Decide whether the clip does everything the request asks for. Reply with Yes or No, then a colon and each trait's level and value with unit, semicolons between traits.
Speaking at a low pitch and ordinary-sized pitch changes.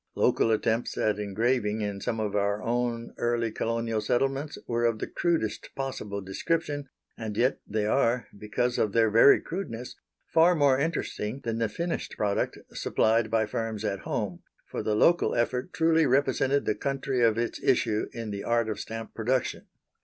Yes: low, 115 Hz; average, 3.5 semitones